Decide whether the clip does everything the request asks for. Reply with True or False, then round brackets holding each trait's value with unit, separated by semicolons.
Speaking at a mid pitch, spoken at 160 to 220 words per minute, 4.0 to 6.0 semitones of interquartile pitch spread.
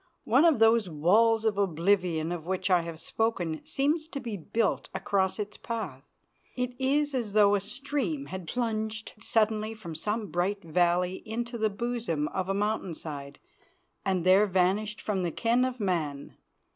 False (205 Hz; 165 wpm; 4.5 semitones)